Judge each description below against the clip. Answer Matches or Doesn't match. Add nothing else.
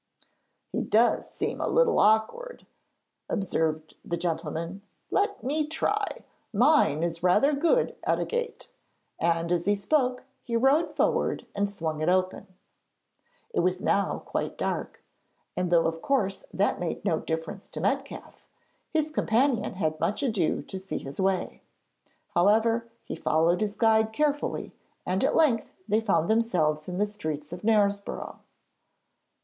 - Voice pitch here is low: Doesn't match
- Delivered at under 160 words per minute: Matches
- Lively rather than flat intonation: Matches